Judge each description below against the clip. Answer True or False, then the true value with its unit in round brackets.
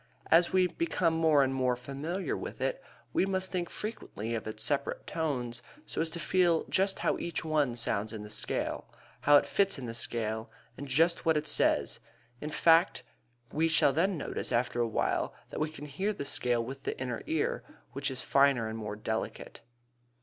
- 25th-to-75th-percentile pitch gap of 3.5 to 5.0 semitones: False (5.5 semitones)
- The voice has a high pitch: False (145 Hz)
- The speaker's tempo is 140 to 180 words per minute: False (195 wpm)